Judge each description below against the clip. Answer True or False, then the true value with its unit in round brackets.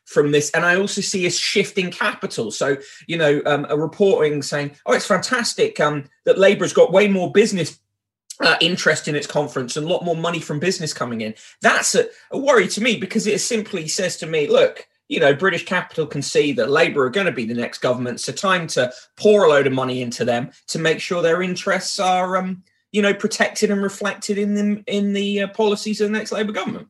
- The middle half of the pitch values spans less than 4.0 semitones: False (5.5 semitones)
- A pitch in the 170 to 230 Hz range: True (185 Hz)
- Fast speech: True (230 wpm)